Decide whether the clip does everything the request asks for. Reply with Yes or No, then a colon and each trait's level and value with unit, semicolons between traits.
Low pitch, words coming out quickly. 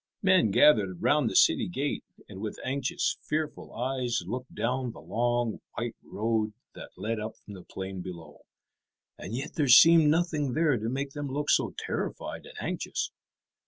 No: low, 125 Hz; average, 165 wpm